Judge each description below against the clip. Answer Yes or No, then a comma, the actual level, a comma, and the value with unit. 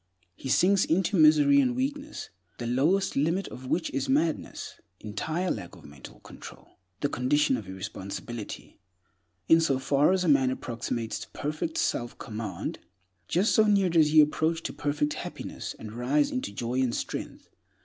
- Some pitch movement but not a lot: No, wide, 5.8 semitones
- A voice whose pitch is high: No, medium, 145 Hz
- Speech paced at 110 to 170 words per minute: Yes, average, 160 wpm